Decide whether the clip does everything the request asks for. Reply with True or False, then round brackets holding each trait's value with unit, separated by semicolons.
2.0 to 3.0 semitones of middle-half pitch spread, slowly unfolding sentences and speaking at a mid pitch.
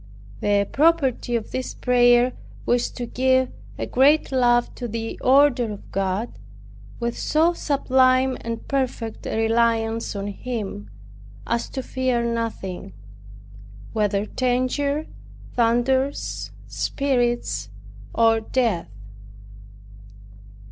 False (2.5 semitones; 100 wpm; 240 Hz)